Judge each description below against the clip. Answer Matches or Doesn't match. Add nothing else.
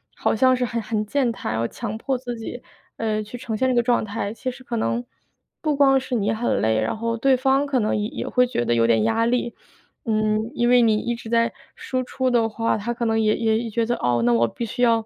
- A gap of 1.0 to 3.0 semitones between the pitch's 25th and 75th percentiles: Matches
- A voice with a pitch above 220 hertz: Matches